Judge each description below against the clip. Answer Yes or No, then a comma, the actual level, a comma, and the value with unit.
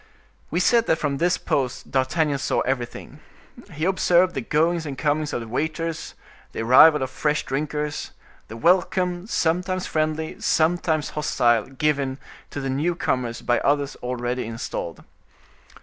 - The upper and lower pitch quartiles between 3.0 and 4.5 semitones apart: Yes, average, 4.0 semitones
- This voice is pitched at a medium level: Yes, medium, 150 Hz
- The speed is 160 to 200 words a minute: No, average, 140 wpm